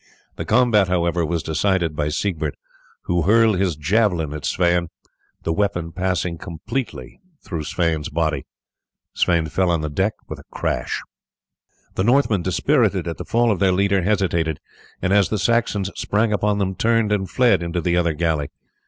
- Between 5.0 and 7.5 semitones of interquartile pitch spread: No, average, 3.8 semitones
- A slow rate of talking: No, average, 165 wpm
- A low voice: Yes, very low, 90 Hz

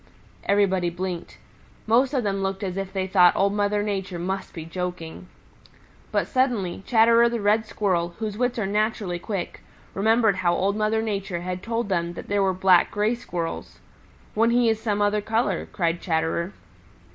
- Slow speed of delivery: No, average, 170 wpm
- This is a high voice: Yes, high, 200 Hz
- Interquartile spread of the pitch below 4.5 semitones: Yes, average, 3.3 semitones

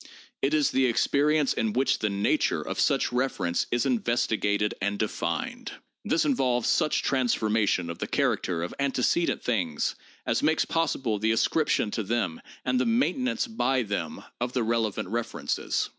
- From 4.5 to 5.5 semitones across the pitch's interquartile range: Yes, average, 5.0 semitones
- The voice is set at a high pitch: No, low, 120 Hz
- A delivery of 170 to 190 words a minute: No, average, 160 wpm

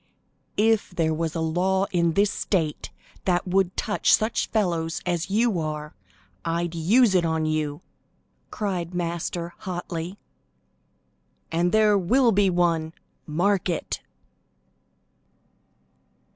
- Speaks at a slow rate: Yes, slow, 115 wpm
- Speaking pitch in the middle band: Yes, medium, 175 Hz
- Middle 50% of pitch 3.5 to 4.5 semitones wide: No, average, 3.1 semitones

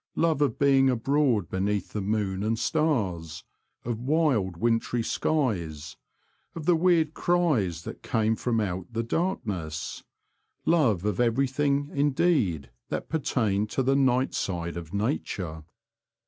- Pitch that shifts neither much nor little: No, wide, 7.1 semitones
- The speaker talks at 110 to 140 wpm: Yes, slow, 135 wpm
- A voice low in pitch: Yes, low, 115 Hz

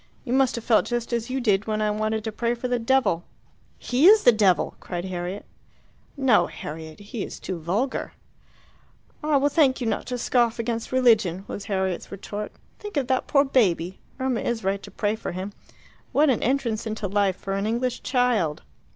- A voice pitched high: Yes, high, 225 Hz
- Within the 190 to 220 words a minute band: Yes, average, 195 wpm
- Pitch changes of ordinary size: Yes, average, 4.3 semitones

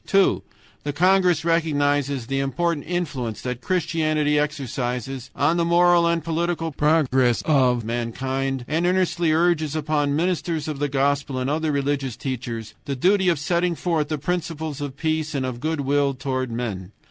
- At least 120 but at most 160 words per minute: Yes, average, 155 wpm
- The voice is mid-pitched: Yes, medium, 145 Hz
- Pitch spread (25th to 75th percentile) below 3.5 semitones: No, average, 3.8 semitones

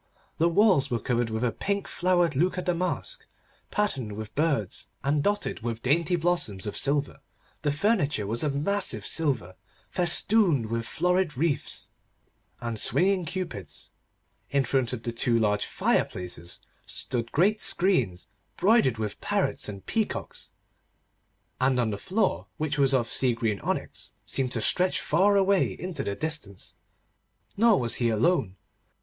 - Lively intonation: Yes, wide, 7.6 semitones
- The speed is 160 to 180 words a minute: No, average, 145 wpm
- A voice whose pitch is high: No, medium, 140 Hz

